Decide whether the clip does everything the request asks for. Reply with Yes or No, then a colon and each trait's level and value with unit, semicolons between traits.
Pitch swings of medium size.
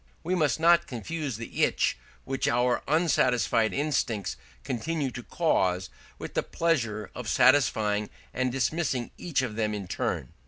No: wide, 6.0 semitones